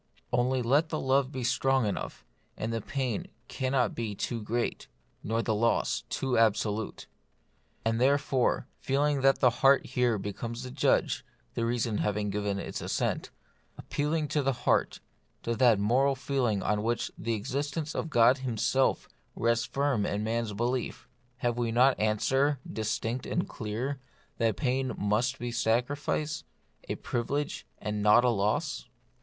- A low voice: Yes, low, 120 Hz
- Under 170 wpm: Yes, average, 145 wpm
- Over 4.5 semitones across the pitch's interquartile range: No, average, 3.2 semitones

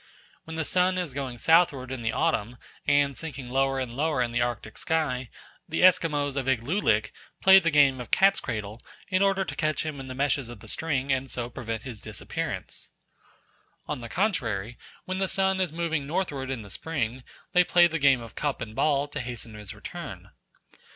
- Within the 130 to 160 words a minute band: No, average, 195 wpm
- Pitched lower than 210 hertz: Yes, medium, 140 Hz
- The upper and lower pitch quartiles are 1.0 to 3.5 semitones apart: No, average, 5.1 semitones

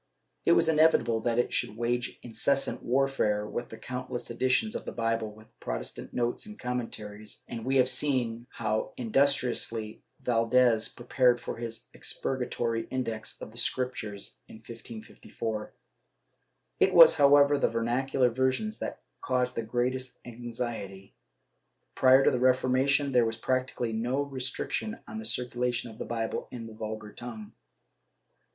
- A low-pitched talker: Yes, low, 120 Hz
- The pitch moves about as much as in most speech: No, narrow, 2.3 semitones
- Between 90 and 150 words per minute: Yes, average, 145 wpm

